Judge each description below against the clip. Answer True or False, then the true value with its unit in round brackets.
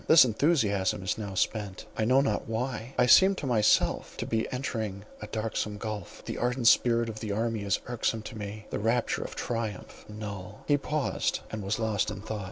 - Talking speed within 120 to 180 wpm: False (195 wpm)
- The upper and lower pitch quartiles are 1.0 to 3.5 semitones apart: True (2.7 semitones)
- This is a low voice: True (110 Hz)